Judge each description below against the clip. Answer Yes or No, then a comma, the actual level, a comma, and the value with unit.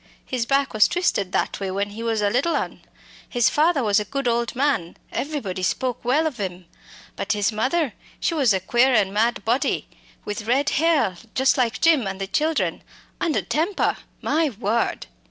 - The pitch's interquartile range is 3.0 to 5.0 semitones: No, wide, 5.5 semitones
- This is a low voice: No, high, 240 Hz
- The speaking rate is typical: Yes, average, 185 wpm